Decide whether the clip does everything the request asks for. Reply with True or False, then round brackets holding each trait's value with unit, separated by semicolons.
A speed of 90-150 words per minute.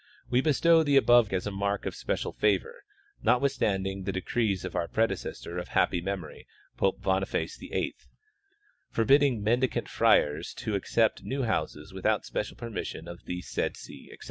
False (160 wpm)